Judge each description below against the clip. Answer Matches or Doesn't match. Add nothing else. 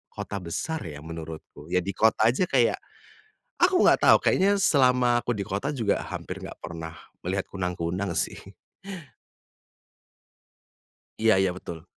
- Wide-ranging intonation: Matches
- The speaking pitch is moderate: Doesn't match